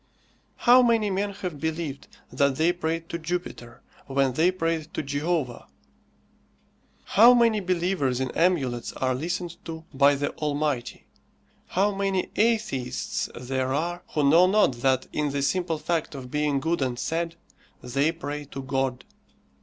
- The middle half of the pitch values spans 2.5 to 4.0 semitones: No, average, 4.6 semitones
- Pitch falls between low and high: Yes, medium, 155 Hz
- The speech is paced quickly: No, average, 145 wpm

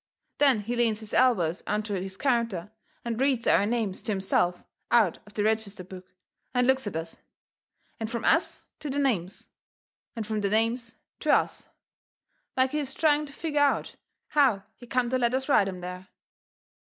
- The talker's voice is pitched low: No, high, 225 Hz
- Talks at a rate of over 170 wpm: Yes, average, 180 wpm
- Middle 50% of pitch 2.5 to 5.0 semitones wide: Yes, average, 4.6 semitones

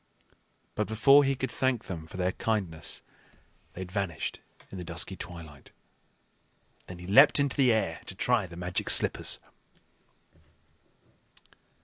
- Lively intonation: Yes, wide, 6.0 semitones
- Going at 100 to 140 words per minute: Yes, slow, 135 wpm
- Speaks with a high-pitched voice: No, very low, 95 Hz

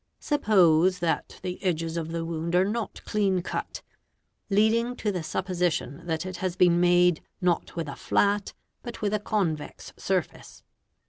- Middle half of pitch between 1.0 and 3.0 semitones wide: No, average, 3.4 semitones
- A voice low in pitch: No, medium, 180 Hz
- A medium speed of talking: Yes, average, 155 wpm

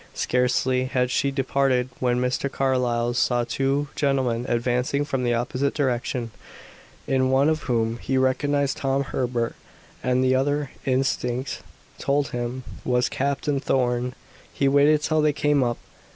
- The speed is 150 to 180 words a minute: No, average, 140 wpm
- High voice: No, low, 130 Hz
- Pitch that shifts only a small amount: Yes, narrow, 2.0 semitones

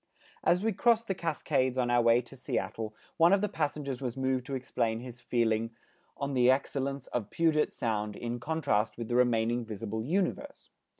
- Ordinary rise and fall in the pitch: Yes, average, 4.6 semitones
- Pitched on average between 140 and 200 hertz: No, low, 125 Hz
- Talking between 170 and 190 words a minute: Yes, average, 180 wpm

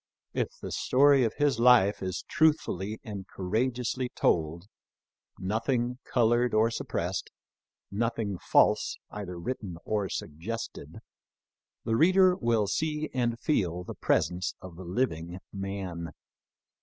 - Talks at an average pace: No, slow, 125 wpm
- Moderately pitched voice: No, low, 110 Hz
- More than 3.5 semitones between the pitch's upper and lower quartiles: Yes, average, 5.0 semitones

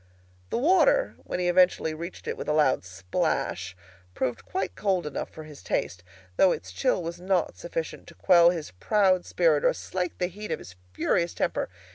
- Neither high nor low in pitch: Yes, medium, 170 Hz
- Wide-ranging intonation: No, average, 3.9 semitones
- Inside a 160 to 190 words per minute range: Yes, average, 185 wpm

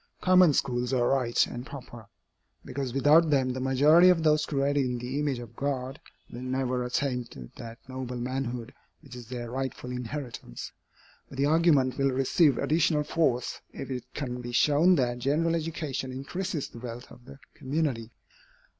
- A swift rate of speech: No, average, 165 wpm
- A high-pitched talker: No, low, 130 Hz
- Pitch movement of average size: Yes, average, 3.0 semitones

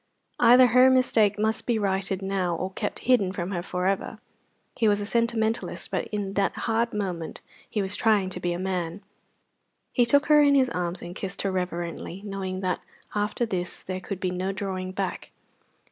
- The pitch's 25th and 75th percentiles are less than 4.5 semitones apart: Yes, average, 3.2 semitones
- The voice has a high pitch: Yes, high, 195 Hz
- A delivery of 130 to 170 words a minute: No, average, 190 wpm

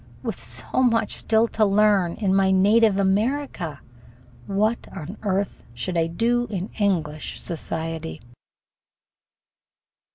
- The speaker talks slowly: Yes, slow, 110 wpm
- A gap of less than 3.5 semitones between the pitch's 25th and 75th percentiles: No, average, 4.4 semitones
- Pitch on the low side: No, high, 195 Hz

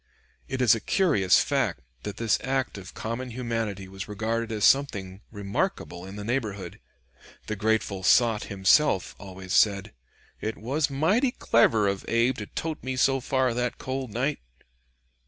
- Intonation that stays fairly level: No, average, 4.7 semitones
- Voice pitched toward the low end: Yes, low, 110 Hz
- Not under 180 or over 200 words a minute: No, average, 155 wpm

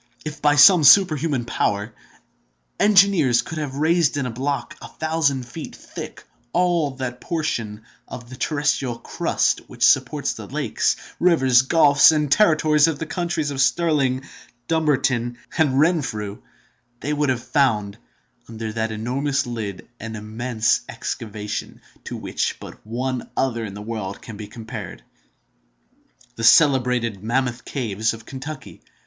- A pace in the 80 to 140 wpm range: Yes, slow, 135 wpm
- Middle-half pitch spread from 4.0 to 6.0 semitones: Yes, average, 4.9 semitones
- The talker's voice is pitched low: Yes, low, 130 Hz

